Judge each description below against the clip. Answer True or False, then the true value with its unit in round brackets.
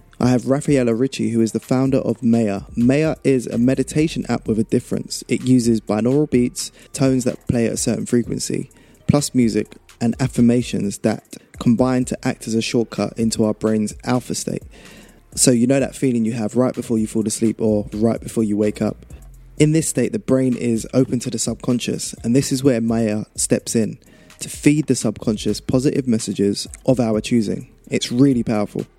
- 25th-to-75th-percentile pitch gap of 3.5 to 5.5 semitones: False (2.7 semitones)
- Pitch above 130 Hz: False (120 Hz)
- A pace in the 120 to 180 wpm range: False (190 wpm)